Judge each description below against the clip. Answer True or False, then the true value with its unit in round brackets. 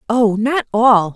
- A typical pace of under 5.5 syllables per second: True (3.4 syllables/s)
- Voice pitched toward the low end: False (230 Hz)